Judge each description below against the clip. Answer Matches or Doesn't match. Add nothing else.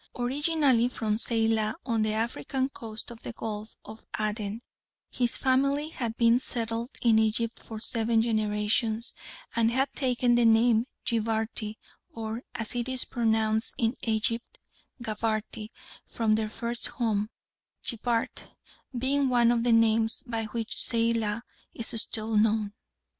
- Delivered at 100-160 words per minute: Matches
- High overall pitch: Matches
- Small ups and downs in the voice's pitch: Matches